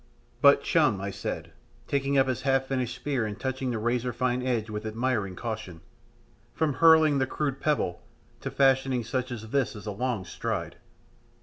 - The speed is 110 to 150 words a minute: No, average, 175 wpm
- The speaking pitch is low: Yes, low, 125 Hz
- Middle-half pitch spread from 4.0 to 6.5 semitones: No, average, 3.5 semitones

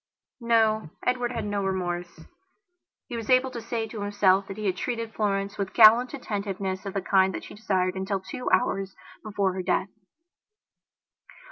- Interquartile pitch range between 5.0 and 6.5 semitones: No, average, 3.0 semitones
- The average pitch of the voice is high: Yes, high, 205 Hz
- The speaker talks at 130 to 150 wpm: No, average, 165 wpm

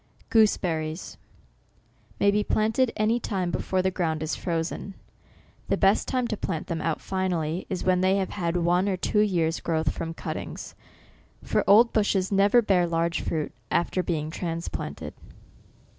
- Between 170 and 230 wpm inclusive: No, average, 160 wpm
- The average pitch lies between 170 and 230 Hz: Yes, medium, 185 Hz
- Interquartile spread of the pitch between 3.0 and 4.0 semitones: Yes, average, 3.4 semitones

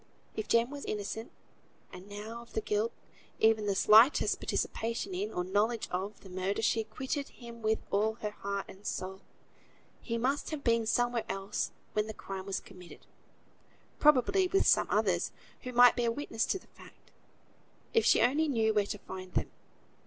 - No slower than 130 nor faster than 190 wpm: Yes, average, 175 wpm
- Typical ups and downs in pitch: Yes, average, 3.1 semitones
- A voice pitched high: Yes, high, 220 Hz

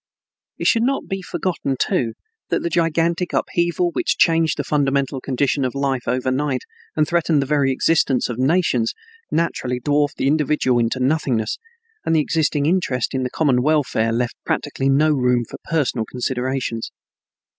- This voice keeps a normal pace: Yes, average, 155 wpm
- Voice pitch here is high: No, medium, 140 Hz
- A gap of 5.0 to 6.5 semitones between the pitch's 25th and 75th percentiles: No, average, 3.9 semitones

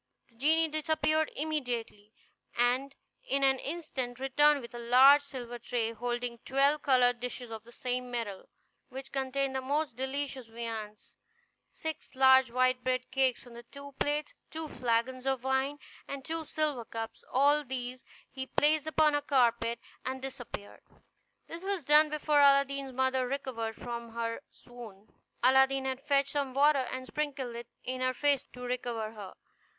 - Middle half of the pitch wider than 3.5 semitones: No, average, 2.7 semitones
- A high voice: Yes, very high, 260 Hz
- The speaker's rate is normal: Yes, average, 155 wpm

